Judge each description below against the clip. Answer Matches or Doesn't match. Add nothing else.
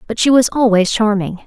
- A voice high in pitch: Matches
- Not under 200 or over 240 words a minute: Matches